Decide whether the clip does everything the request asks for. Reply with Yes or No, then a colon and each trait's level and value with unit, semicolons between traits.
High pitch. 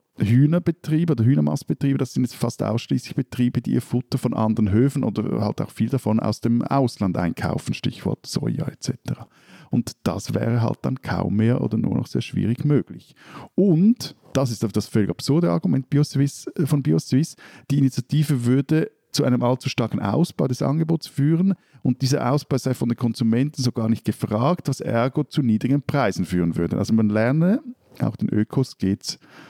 No: low, 130 Hz